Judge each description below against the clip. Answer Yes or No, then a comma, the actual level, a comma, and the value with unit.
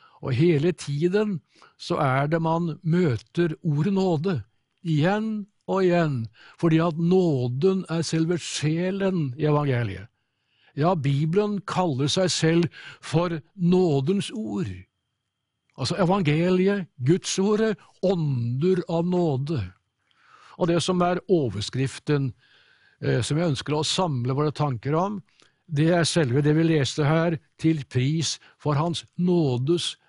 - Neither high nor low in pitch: Yes, medium, 160 Hz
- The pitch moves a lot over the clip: No, average, 4.5 semitones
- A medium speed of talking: No, slow, 120 wpm